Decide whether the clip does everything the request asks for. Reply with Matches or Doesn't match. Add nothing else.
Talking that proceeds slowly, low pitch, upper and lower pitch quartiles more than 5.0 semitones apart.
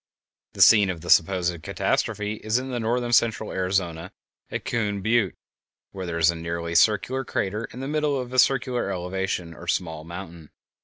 Doesn't match